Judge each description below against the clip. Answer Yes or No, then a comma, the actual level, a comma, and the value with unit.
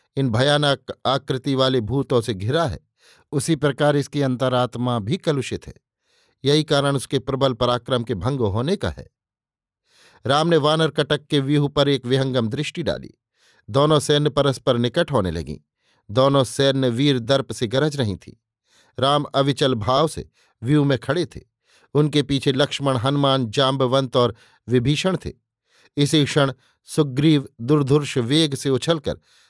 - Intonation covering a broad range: No, narrow, 2.5 semitones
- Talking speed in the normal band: Yes, average, 150 wpm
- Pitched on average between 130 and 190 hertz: Yes, low, 135 Hz